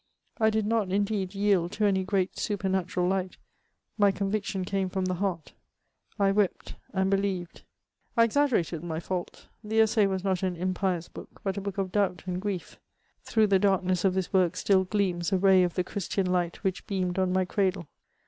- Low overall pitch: No, high, 190 Hz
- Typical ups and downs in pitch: No, narrow, 1.8 semitones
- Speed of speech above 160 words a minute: Yes, average, 185 wpm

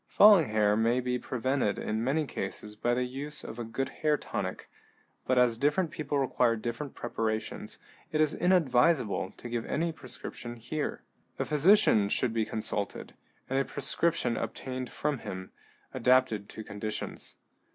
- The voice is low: Yes, low, 125 Hz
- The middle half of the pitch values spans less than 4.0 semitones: No, average, 4.7 semitones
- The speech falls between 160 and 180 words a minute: No, average, 150 wpm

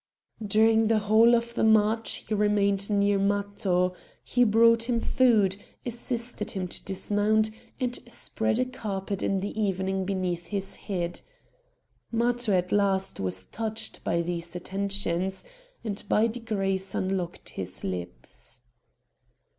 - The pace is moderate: No, slow, 130 wpm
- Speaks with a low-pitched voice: No, high, 200 Hz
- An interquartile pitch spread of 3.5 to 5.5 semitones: No, average, 2.8 semitones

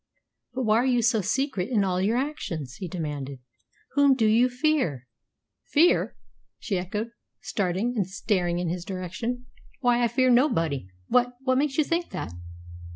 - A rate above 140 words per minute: Yes, average, 160 wpm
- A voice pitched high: Yes, high, 220 Hz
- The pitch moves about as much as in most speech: No, wide, 6.1 semitones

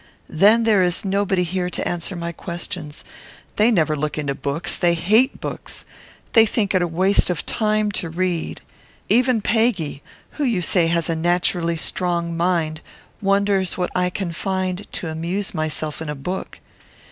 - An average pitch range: Yes, average, 3.2 semitones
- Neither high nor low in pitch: Yes, medium, 180 Hz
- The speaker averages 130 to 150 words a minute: No, average, 160 wpm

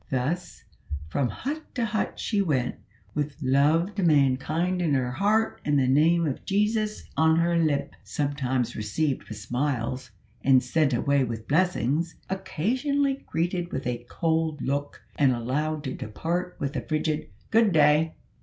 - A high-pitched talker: No, medium, 150 Hz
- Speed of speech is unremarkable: Yes, average, 150 wpm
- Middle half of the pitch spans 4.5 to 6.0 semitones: Yes, average, 4.9 semitones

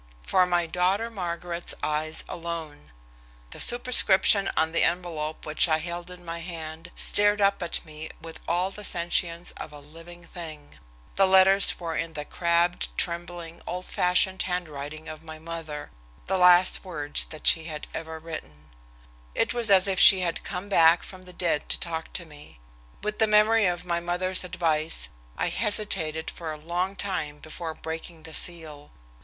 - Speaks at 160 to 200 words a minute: Yes, average, 170 wpm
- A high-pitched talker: No, medium, 170 Hz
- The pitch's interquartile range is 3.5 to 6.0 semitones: No, narrow, 2.4 semitones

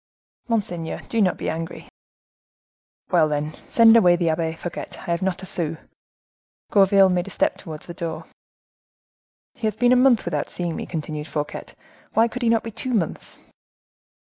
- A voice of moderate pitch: Yes, medium, 180 Hz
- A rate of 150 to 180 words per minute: Yes, average, 170 wpm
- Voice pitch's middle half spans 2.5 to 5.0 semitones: No, wide, 5.4 semitones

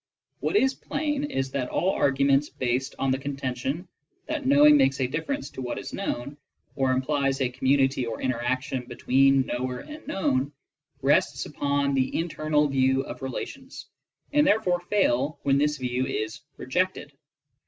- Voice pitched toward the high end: No, low, 135 Hz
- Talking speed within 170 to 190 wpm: No, average, 155 wpm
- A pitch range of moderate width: Yes, average, 5.0 semitones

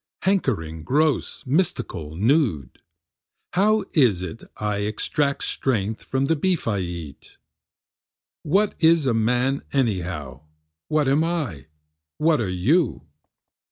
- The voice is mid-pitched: No, low, 125 Hz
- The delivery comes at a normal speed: No, slow, 115 wpm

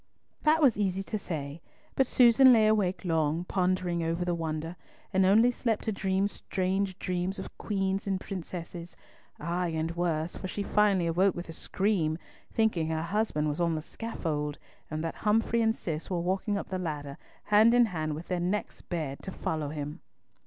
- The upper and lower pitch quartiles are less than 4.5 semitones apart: Yes, average, 3.9 semitones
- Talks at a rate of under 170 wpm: No, average, 180 wpm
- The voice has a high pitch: No, medium, 180 Hz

